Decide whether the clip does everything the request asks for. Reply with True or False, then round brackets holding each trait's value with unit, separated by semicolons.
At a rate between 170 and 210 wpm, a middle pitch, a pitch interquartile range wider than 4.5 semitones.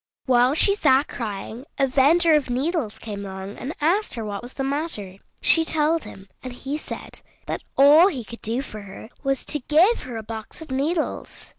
False (195 wpm; 265 Hz; 5.5 semitones)